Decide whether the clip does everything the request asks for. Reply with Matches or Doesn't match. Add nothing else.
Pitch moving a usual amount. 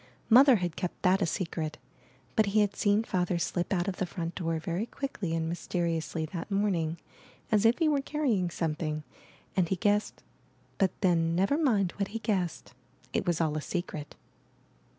Matches